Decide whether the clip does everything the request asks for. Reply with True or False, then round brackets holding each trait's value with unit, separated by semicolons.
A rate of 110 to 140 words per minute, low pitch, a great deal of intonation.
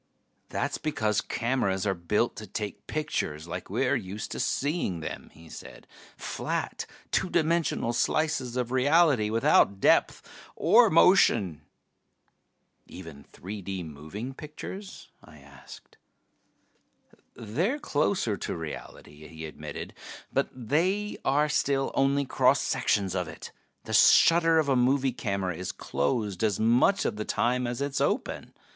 True (135 wpm; 115 Hz; 7.2 semitones)